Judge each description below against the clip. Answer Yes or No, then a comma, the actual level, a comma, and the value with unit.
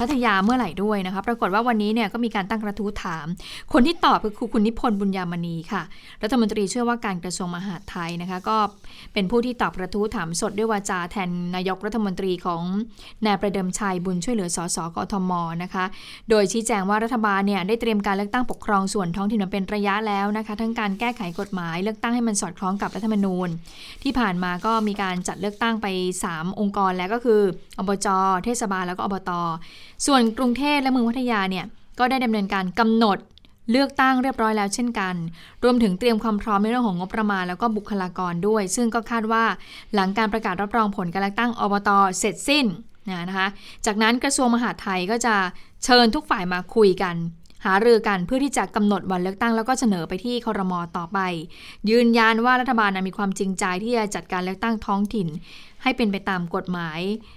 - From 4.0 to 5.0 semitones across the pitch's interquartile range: No, average, 3.4 semitones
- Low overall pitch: No, high, 205 Hz